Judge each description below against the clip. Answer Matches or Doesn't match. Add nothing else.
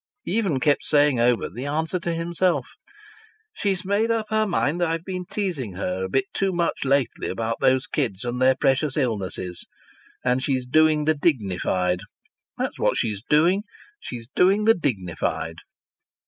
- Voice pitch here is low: Doesn't match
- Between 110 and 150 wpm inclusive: Doesn't match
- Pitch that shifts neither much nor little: Doesn't match